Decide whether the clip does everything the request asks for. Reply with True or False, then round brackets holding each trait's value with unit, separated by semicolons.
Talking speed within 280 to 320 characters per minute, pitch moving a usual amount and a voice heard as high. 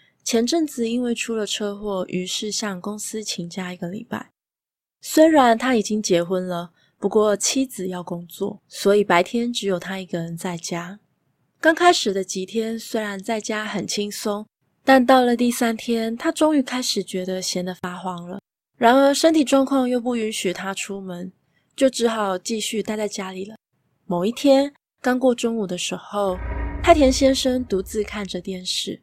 False (250 characters per minute; 4.6 semitones; 210 Hz)